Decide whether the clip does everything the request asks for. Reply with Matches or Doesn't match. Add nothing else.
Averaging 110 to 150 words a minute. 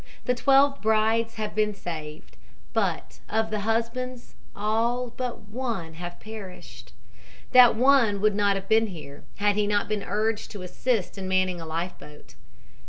Doesn't match